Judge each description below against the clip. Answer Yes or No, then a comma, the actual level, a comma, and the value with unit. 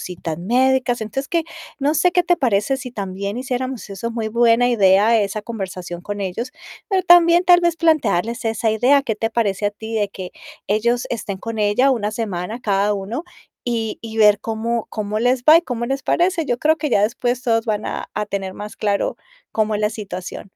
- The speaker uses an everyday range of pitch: Yes, average, 3.8 semitones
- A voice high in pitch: Yes, high, 225 Hz